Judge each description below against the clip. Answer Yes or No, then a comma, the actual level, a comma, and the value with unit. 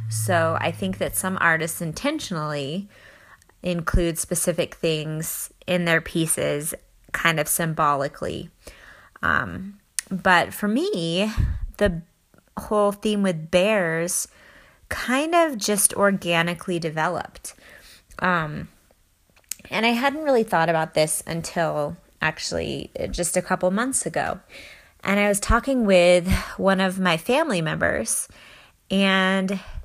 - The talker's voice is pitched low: No, medium, 180 Hz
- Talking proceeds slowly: Yes, slow, 115 wpm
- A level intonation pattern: No, average, 3.6 semitones